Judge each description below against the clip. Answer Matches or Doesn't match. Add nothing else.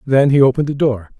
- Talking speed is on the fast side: Matches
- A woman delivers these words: Doesn't match